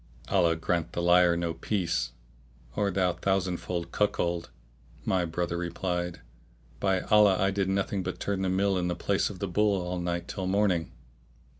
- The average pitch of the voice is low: Yes, very low, 90 Hz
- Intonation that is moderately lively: No, narrow, 2.0 semitones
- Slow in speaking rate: No, average, 165 wpm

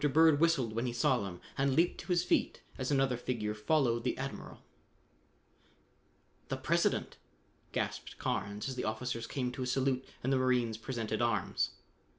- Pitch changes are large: No, average, 2.8 semitones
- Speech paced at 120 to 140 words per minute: No, average, 165 wpm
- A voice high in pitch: No, low, 125 Hz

